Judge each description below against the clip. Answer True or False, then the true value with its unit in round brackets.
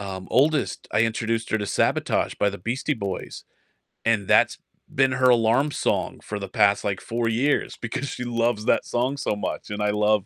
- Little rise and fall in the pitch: False (3.1 semitones)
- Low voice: True (115 Hz)